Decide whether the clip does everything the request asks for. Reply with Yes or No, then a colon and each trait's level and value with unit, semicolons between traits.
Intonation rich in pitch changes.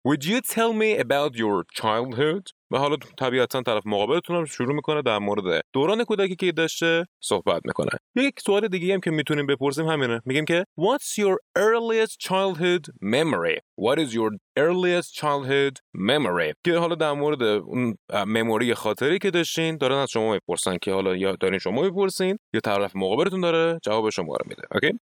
Yes: wide, 7.3 semitones